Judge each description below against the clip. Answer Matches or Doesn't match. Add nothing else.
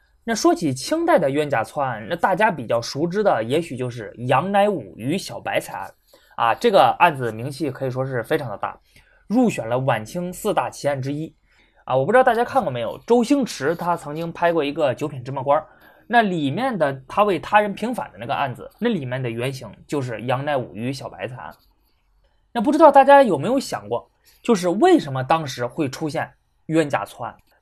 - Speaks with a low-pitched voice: Doesn't match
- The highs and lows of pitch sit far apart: Matches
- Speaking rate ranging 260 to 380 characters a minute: Matches